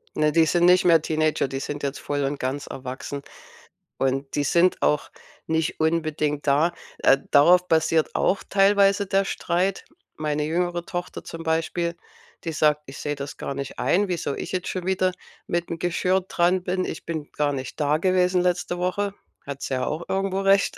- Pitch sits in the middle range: Yes, medium, 165 Hz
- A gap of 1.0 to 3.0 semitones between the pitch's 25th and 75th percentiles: No, average, 3.6 semitones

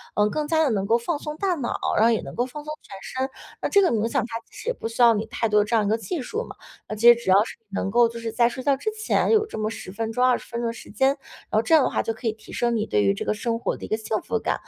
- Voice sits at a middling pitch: No, high, 230 Hz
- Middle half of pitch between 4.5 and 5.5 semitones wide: No, average, 3.8 semitones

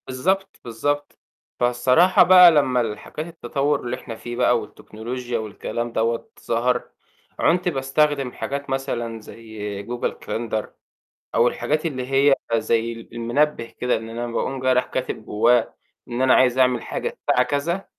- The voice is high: No, low, 125 Hz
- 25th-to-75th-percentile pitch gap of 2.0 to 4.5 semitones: Yes, average, 3.3 semitones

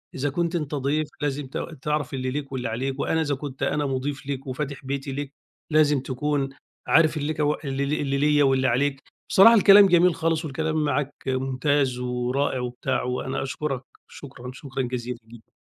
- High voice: No, medium, 140 Hz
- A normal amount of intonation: No, narrow, 2.3 semitones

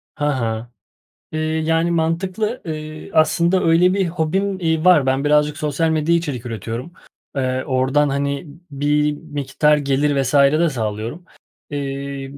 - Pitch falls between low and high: Yes, medium, 150 Hz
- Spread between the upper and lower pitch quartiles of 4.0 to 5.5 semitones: No, average, 3.1 semitones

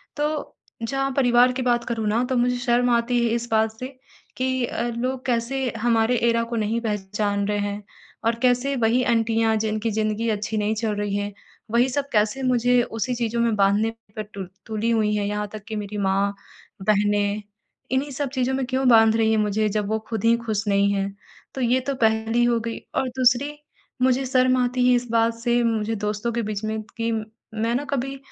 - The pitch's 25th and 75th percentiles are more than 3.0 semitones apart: No, average, 2.7 semitones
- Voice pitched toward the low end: No, high, 230 Hz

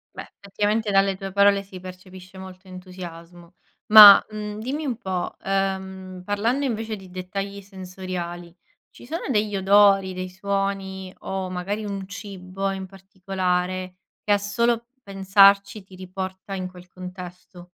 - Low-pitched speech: No, high, 190 Hz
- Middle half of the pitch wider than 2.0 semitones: No, narrow, 1.6 semitones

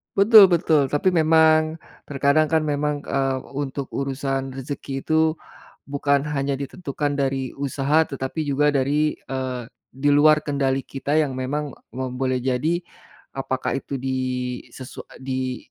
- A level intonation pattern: Yes, narrow, 2.2 semitones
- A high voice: No, medium, 140 Hz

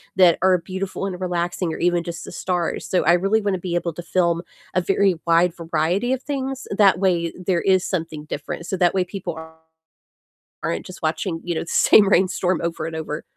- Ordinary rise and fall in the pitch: No, narrow, 2.0 semitones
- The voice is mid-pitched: Yes, medium, 180 Hz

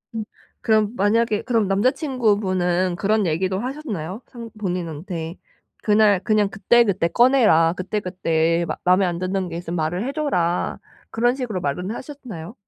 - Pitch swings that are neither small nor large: Yes, average, 4.6 semitones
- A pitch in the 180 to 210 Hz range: Yes, high, 195 Hz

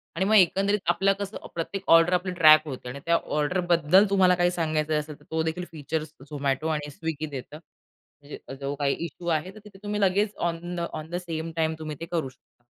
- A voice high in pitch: No, medium, 165 Hz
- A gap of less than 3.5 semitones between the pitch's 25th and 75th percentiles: Yes, average, 3.0 semitones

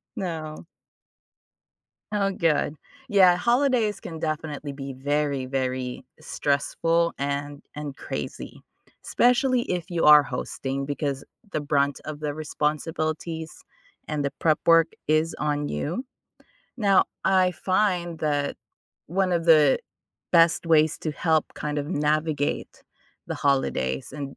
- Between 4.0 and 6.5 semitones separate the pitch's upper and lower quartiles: No, average, 3.0 semitones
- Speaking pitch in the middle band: Yes, medium, 155 Hz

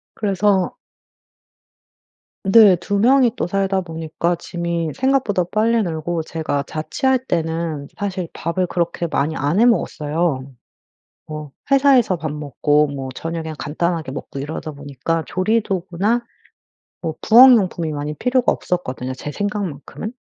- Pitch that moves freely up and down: No, average, 4.8 semitones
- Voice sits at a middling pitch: Yes, medium, 170 Hz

